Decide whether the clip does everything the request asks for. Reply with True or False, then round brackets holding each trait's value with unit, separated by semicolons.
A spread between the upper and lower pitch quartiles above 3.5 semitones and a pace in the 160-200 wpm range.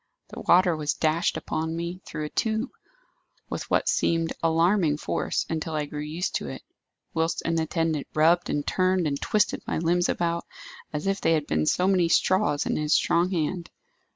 False (2.6 semitones; 180 wpm)